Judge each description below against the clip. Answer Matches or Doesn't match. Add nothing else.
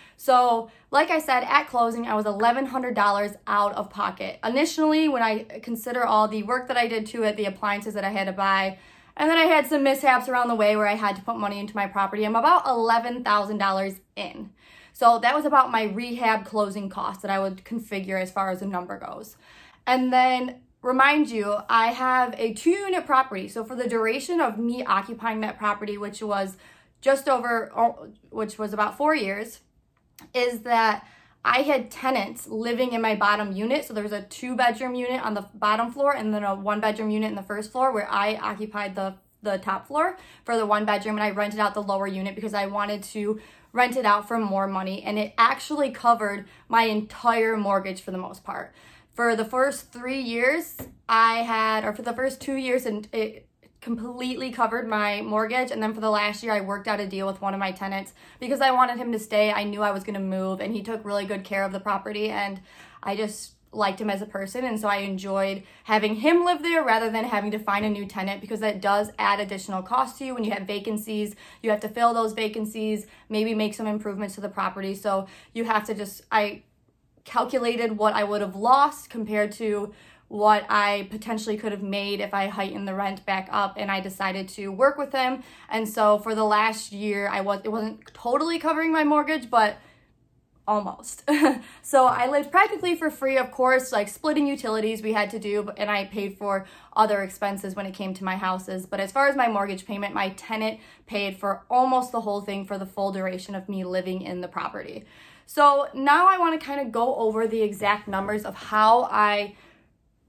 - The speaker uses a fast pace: Matches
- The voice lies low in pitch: Doesn't match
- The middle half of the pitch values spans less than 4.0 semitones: Matches